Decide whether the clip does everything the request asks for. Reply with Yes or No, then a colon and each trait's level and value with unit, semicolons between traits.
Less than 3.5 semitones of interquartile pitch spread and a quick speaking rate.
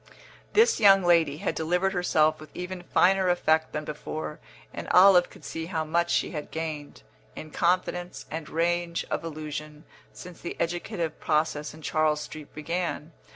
No: narrow, 2.5 semitones; average, 155 wpm